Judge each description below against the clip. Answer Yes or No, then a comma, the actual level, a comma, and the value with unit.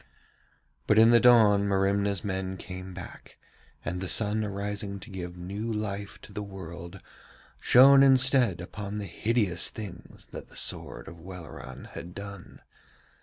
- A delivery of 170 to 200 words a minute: No, average, 145 wpm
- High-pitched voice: No, low, 100 Hz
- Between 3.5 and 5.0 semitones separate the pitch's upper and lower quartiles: No, average, 2.7 semitones